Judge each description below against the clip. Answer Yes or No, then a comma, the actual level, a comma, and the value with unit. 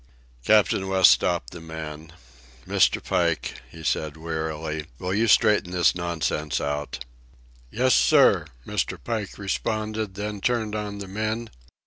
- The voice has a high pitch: No, very low, 95 Hz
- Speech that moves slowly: Yes, slow, 130 wpm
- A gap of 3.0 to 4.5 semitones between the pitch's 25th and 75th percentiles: No, average, 5.2 semitones